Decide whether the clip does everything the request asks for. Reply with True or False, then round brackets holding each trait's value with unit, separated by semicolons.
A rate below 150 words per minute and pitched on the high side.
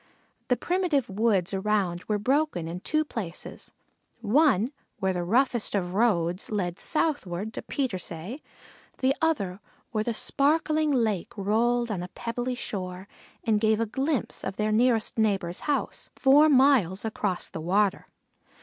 True (140 wpm; 220 Hz)